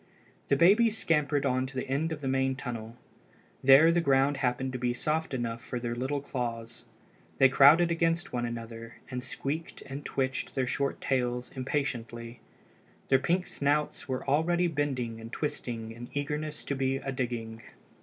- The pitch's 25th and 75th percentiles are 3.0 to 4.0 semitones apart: Yes, average, 3.3 semitones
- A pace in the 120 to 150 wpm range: No, average, 165 wpm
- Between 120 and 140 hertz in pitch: Yes, low, 135 Hz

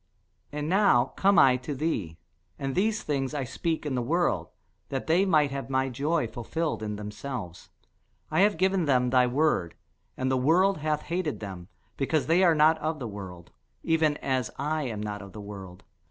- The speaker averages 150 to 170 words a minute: No, average, 185 wpm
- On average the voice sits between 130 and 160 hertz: Yes, medium, 140 Hz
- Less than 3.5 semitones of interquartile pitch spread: No, average, 5.3 semitones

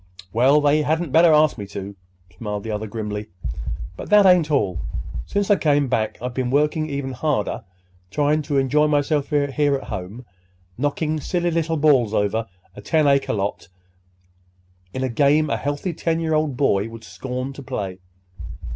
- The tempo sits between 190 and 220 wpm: No, average, 165 wpm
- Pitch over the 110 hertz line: Yes, medium, 140 Hz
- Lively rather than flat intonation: Yes, wide, 5.7 semitones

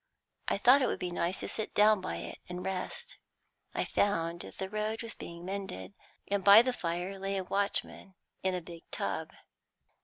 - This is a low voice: No, high, 190 Hz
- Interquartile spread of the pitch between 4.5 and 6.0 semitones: No, average, 3.0 semitones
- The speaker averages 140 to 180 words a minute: No, average, 190 wpm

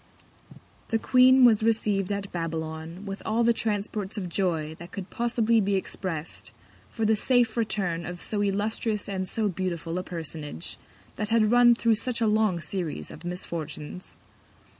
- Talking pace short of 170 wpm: Yes, average, 160 wpm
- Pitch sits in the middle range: No, high, 200 Hz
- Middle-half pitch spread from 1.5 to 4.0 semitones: No, average, 4.4 semitones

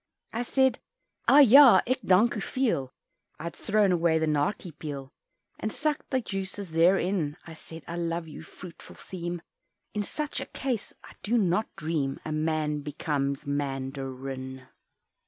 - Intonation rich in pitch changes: Yes, wide, 6.1 semitones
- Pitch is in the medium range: Yes, medium, 170 Hz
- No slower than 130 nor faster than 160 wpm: Yes, average, 155 wpm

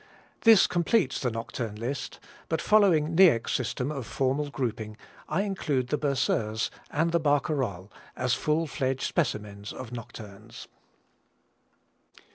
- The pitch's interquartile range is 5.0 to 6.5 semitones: Yes, wide, 5.4 semitones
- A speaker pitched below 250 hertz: Yes, low, 135 Hz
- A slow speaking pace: Yes, slow, 115 wpm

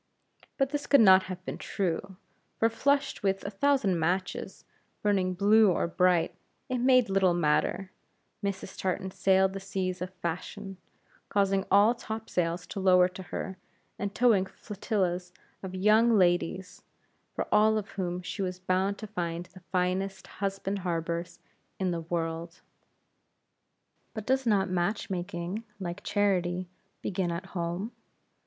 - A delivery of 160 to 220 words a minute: No, average, 140 wpm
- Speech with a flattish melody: Yes, narrow, 2.2 semitones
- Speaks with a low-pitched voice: No, high, 190 Hz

